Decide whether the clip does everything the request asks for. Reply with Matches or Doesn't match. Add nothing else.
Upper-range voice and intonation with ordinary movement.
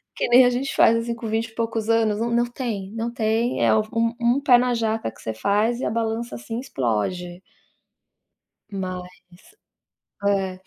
Matches